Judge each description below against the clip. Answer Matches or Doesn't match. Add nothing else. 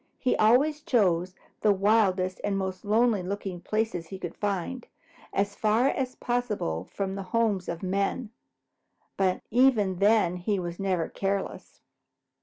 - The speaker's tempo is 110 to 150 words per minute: Matches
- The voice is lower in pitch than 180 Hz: Doesn't match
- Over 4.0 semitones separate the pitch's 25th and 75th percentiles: Doesn't match